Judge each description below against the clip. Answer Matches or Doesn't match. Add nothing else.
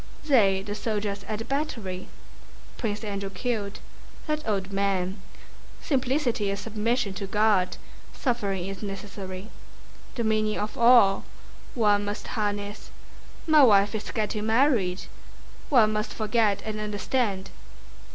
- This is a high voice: Matches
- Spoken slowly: Matches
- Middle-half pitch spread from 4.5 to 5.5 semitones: Doesn't match